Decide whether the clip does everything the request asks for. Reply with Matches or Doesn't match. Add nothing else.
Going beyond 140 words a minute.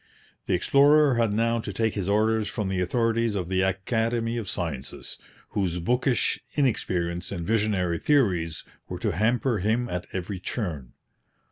Matches